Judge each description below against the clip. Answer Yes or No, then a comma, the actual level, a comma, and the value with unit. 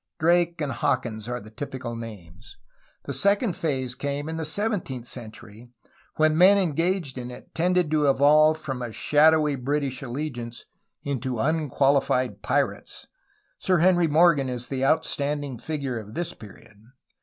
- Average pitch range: Yes, average, 4.5 semitones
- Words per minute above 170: No, average, 150 wpm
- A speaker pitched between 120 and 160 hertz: Yes, medium, 140 Hz